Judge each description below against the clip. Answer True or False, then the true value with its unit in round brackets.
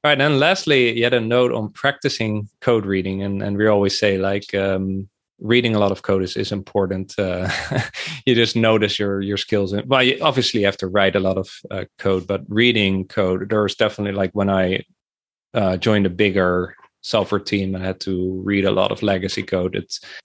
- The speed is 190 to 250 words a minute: True (205 wpm)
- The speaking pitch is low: True (100 Hz)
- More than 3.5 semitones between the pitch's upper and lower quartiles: False (2.7 semitones)